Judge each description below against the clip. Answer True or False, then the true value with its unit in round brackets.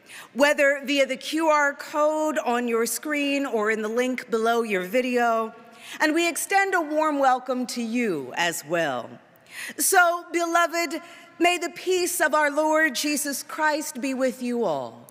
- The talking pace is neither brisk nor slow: True (155 wpm)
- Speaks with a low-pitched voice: False (285 Hz)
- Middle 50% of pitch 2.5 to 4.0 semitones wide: False (4.7 semitones)